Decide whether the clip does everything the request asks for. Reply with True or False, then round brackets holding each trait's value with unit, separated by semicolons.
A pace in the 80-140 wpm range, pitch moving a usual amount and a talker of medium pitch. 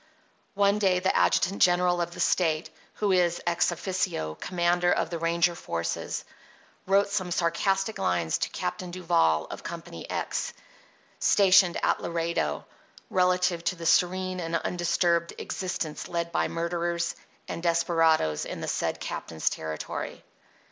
False (135 wpm; 1.6 semitones; 175 Hz)